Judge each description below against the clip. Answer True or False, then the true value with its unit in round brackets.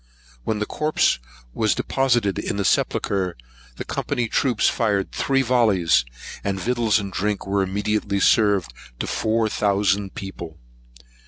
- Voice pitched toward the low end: True (105 Hz)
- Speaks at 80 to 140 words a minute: True (135 wpm)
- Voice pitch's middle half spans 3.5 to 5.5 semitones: False (2.7 semitones)